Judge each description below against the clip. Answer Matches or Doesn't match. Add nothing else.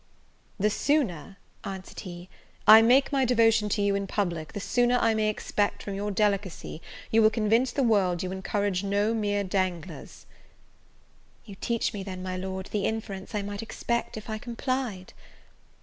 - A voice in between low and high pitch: Doesn't match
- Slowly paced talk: Doesn't match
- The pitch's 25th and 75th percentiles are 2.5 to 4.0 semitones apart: Matches